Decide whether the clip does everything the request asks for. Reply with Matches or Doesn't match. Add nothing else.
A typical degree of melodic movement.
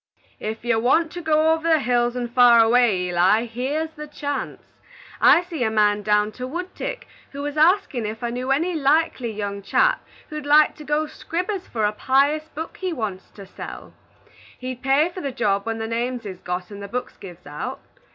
Doesn't match